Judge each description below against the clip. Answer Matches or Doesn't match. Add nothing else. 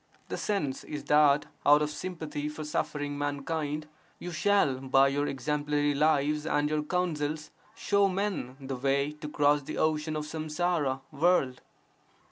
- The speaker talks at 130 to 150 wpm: Matches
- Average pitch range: Doesn't match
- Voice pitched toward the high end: Doesn't match